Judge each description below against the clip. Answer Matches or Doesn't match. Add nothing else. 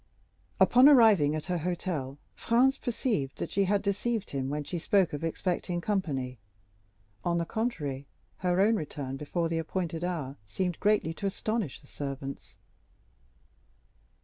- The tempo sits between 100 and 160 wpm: Matches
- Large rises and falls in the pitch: Matches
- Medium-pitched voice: Matches